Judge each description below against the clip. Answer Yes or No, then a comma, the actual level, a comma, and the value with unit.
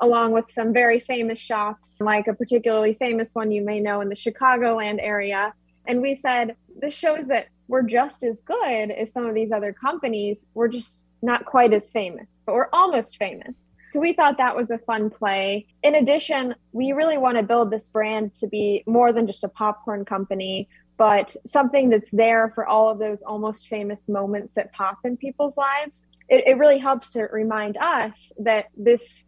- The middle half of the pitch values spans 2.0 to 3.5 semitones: Yes, average, 3.0 semitones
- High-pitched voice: Yes, high, 225 Hz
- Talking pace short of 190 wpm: No, average, 195 wpm